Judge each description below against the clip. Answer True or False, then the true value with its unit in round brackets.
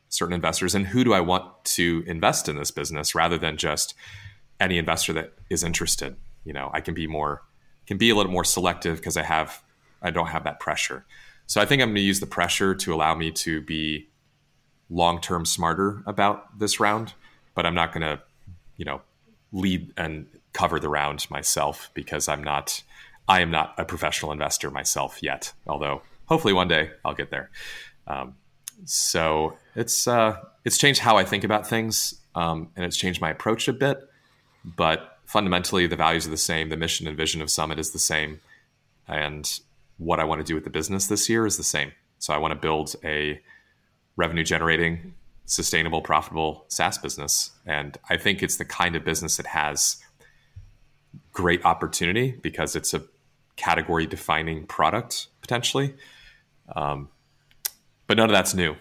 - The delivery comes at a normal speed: True (180 wpm)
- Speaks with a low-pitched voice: True (85 Hz)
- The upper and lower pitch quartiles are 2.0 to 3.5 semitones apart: False (4.6 semitones)